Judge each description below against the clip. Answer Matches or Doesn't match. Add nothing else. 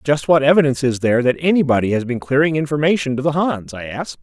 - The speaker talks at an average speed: Doesn't match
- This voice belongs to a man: Matches